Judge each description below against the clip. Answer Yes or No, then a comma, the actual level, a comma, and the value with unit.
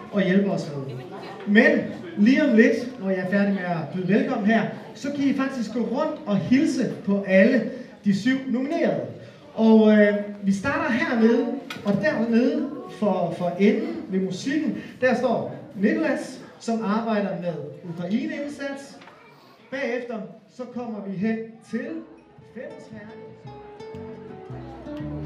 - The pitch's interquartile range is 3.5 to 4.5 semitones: Yes, average, 4.1 semitones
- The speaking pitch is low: No, high, 220 Hz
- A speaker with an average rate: No, slow, 135 wpm